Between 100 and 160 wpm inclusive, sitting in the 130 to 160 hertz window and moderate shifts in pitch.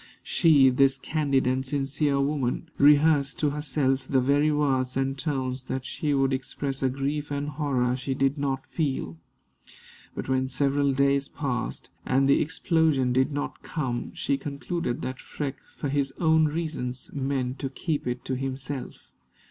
No: average, 155 wpm; low, 135 Hz; narrow, 1.8 semitones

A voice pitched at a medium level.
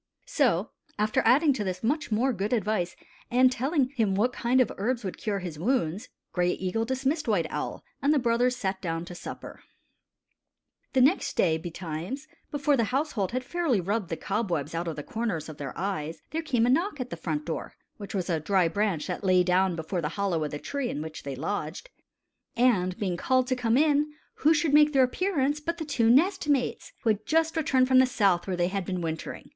No: high, 220 Hz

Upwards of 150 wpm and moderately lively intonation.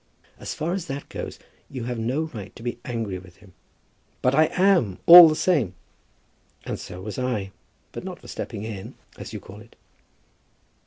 No: average, 180 wpm; wide, 7.3 semitones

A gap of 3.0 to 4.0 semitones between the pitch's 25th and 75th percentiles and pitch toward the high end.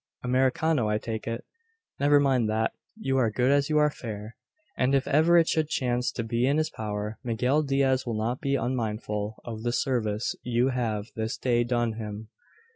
No: average, 3.6 semitones; low, 120 Hz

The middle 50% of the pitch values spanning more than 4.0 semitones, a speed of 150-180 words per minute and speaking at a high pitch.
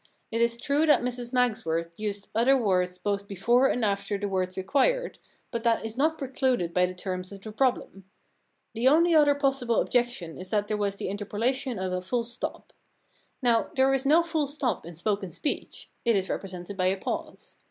No: wide, 5.4 semitones; fast, 205 wpm; high, 225 Hz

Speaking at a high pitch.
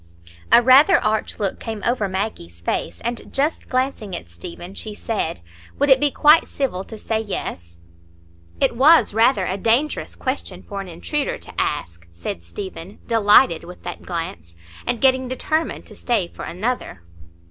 Yes: high, 215 Hz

